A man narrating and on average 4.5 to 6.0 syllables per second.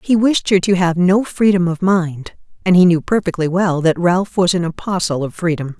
No: female; 5.0 syllables/s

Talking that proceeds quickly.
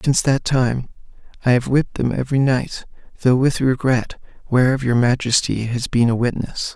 No: average, 170 wpm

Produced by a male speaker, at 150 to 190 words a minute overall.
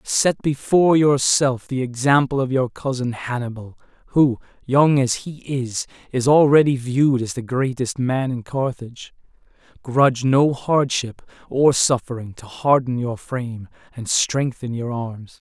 No: male; average, 140 wpm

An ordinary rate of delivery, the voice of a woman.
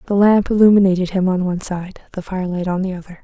No: fast, 220 wpm; female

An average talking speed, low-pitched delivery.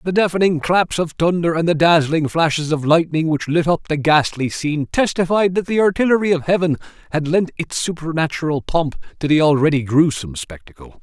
No: average, 180 wpm; medium, 160 Hz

